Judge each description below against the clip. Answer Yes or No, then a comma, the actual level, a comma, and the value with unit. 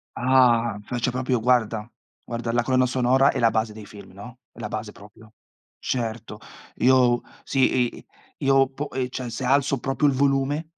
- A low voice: Yes, low, 125 Hz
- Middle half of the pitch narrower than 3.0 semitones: Yes, narrow, 2.5 semitones